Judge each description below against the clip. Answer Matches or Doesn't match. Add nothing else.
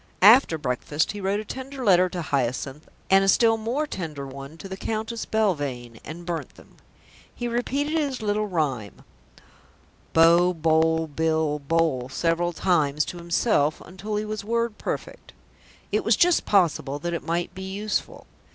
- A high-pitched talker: Doesn't match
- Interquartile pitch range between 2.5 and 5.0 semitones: Doesn't match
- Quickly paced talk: Doesn't match